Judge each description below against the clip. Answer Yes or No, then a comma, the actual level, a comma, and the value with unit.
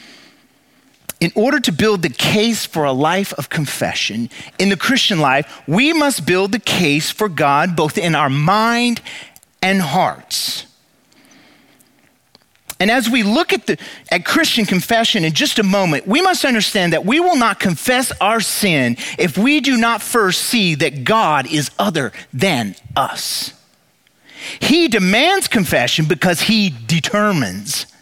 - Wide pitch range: Yes, wide, 6.7 semitones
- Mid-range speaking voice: No, high, 205 Hz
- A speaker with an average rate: Yes, average, 150 wpm